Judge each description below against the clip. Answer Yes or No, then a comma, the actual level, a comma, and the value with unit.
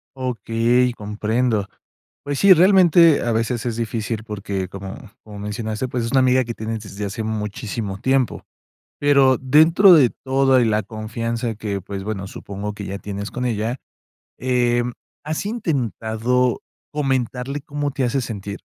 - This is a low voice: Yes, low, 115 Hz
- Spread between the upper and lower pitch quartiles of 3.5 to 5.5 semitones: Yes, average, 3.8 semitones